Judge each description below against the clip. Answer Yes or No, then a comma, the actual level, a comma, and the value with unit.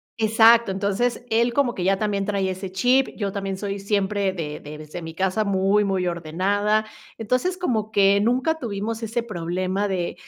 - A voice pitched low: No, high, 200 Hz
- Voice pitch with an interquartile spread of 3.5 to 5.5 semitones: No, average, 2.9 semitones